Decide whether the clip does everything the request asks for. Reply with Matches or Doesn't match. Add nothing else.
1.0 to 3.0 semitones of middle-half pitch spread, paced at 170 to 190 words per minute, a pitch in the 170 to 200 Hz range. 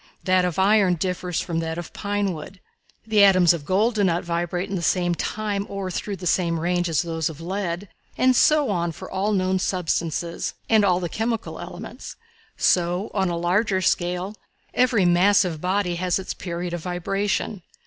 Matches